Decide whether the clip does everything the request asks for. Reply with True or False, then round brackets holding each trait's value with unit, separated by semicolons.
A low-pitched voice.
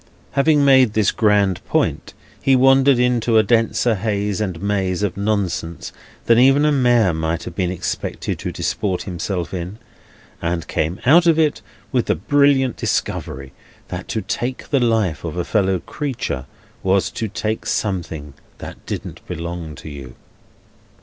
True (105 Hz)